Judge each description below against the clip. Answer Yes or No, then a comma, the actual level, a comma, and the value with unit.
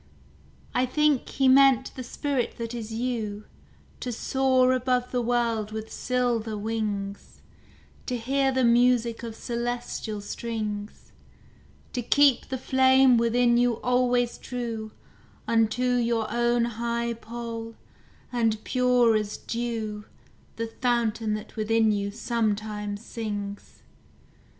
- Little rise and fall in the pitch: Yes, narrow, 2.2 semitones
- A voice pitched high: Yes, high, 235 Hz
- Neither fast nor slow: No, slow, 115 wpm